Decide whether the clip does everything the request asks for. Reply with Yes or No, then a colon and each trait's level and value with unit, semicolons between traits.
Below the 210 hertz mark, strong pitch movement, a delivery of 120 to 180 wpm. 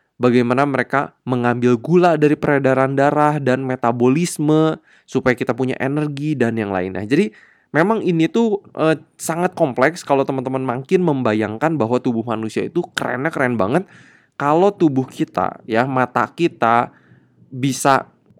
No: low, 135 Hz; average, 4.2 semitones; average, 135 wpm